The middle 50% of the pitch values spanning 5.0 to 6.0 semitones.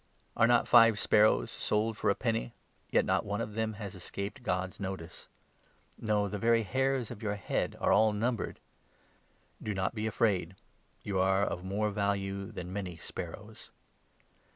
No: narrow, 2.6 semitones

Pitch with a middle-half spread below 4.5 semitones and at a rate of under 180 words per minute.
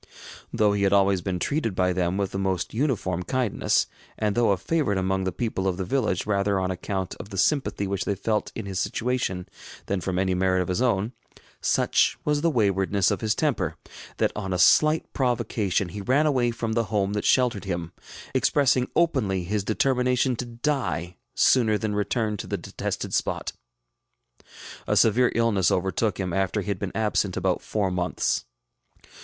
No: average, 4.1 semitones; average, 185 wpm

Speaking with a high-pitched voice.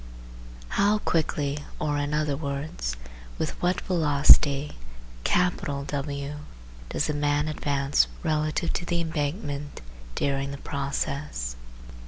No: medium, 145 Hz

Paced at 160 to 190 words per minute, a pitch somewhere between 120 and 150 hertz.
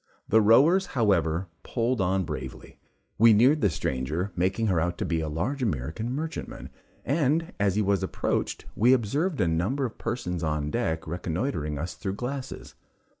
No: average, 165 wpm; low, 100 Hz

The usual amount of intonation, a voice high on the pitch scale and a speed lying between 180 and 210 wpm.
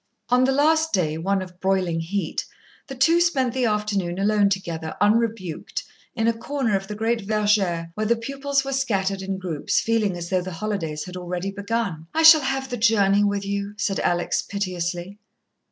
Yes: average, 4.1 semitones; high, 200 Hz; average, 185 wpm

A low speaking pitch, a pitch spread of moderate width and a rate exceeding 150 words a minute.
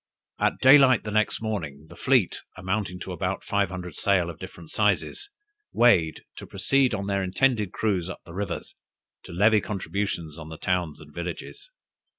Yes: very low, 95 Hz; average, 3.8 semitones; average, 170 wpm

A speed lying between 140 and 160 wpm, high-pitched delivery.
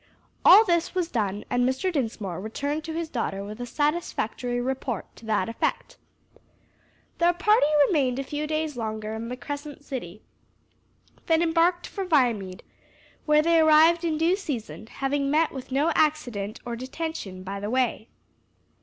Yes: average, 155 wpm; very high, 275 Hz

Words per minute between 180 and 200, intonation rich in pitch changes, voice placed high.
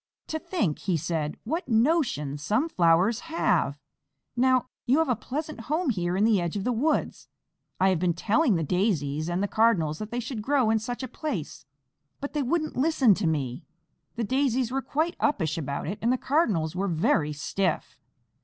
Yes: average, 190 wpm; wide, 8.1 semitones; high, 220 Hz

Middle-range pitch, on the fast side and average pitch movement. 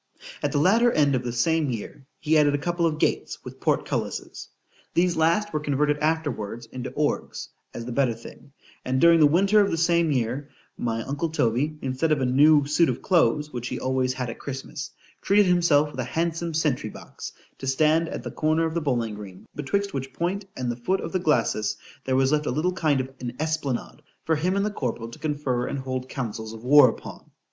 Yes: medium, 145 Hz; fast, 215 wpm; average, 4.3 semitones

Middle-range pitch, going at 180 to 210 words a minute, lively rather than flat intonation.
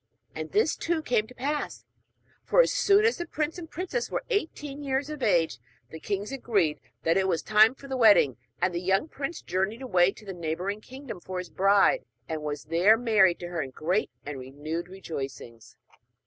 No: high, 205 Hz; average, 195 wpm; wide, 8.0 semitones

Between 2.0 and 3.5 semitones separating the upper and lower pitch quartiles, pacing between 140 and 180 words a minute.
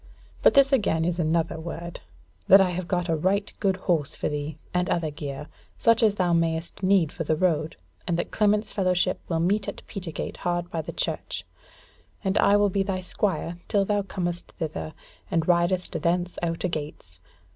No: average, 2.9 semitones; average, 190 wpm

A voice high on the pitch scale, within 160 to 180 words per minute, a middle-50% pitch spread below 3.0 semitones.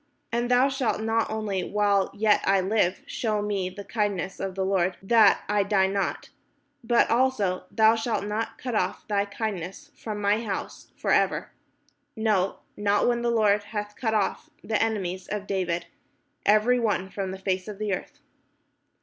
Yes: high, 210 Hz; average, 170 wpm; narrow, 2.5 semitones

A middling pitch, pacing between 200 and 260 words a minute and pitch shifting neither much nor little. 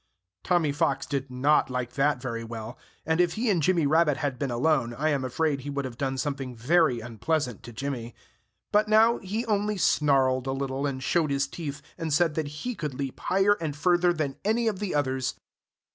Yes: medium, 145 Hz; fast, 205 wpm; average, 4.5 semitones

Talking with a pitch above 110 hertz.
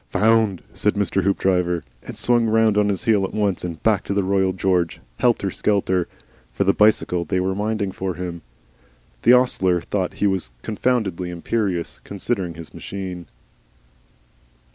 No: very low, 95 Hz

